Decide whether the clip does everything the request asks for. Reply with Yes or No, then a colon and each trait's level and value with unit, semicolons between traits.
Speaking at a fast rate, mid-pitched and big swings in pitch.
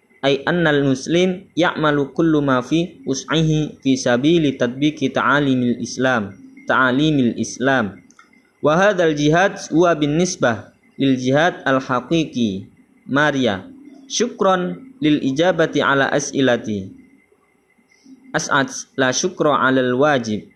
No: average, 90 wpm; medium, 150 Hz; wide, 5.7 semitones